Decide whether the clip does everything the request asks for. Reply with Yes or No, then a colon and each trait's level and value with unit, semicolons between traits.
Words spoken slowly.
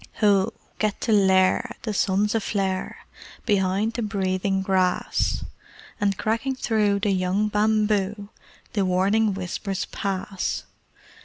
Yes: slow, 110 wpm